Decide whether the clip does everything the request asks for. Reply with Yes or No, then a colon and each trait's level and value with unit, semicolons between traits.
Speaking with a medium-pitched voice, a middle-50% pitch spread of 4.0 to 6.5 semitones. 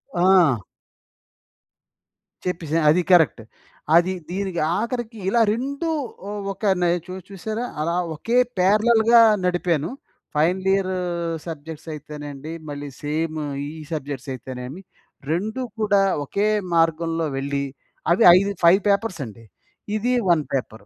Yes: medium, 175 Hz; average, 5.0 semitones